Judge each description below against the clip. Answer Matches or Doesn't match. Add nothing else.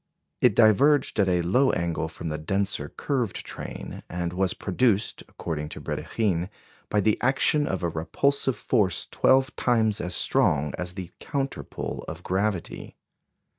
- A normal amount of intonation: Doesn't match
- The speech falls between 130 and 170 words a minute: Matches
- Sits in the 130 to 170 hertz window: Doesn't match